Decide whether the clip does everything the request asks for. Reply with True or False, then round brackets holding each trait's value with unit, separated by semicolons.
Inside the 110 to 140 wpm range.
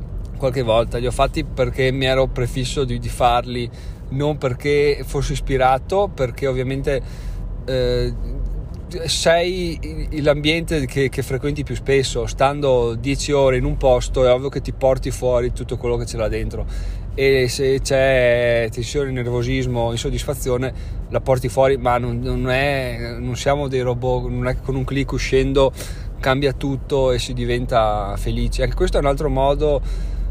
False (160 wpm)